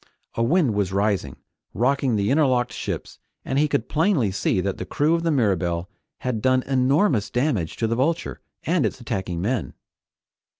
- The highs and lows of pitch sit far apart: Yes, wide, 6.0 semitones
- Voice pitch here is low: Yes, low, 120 Hz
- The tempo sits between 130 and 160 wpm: No, average, 170 wpm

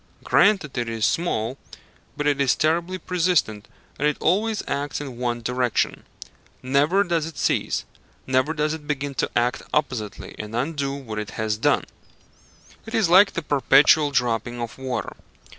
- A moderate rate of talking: Yes, average, 160 wpm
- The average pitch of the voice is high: No, medium, 140 Hz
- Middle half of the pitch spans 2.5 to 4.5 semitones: No, average, 5.1 semitones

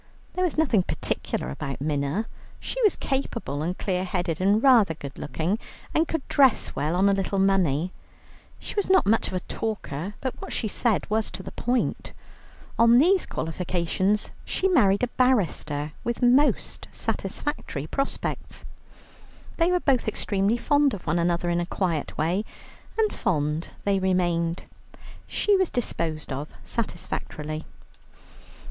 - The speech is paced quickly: No, average, 150 wpm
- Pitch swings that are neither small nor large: No, wide, 6.9 semitones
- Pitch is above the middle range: Yes, high, 195 Hz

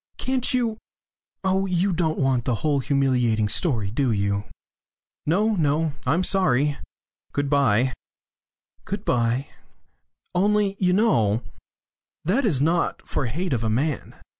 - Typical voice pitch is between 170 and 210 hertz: No, medium, 145 Hz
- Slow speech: Yes, slow, 130 wpm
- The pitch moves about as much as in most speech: No, wide, 7.3 semitones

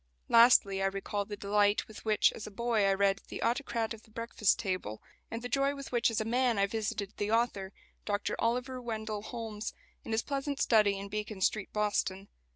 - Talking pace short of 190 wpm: No, average, 200 wpm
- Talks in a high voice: Yes, high, 215 Hz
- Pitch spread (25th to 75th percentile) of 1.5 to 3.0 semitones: Yes, narrow, 2.6 semitones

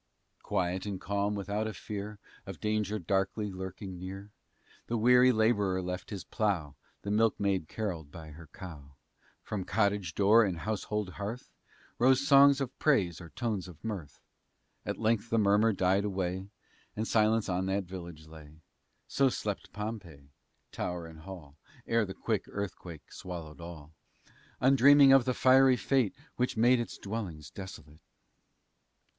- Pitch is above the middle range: No, low, 100 Hz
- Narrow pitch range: No, average, 3.9 semitones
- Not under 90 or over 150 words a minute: Yes, average, 145 wpm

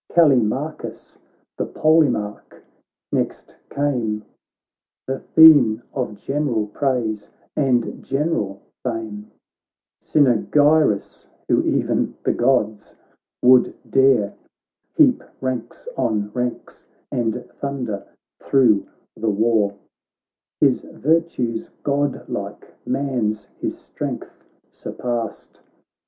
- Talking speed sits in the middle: No, slow, 85 wpm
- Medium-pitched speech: No, low, 125 Hz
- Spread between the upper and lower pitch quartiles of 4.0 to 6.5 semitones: Yes, average, 4.5 semitones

